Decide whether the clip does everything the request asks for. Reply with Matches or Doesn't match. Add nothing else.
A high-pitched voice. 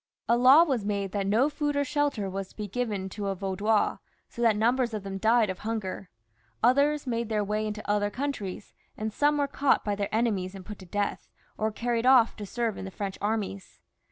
Matches